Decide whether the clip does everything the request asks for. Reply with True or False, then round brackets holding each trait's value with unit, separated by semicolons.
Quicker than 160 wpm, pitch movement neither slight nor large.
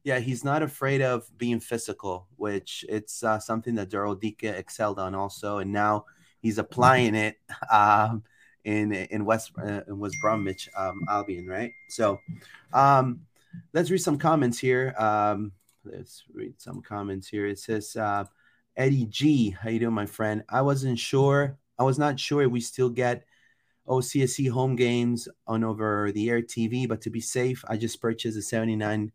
True (170 wpm; 3.4 semitones)